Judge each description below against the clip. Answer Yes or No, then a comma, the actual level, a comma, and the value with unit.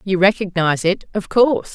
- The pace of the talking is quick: No, average, 170 wpm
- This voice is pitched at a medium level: No, high, 195 Hz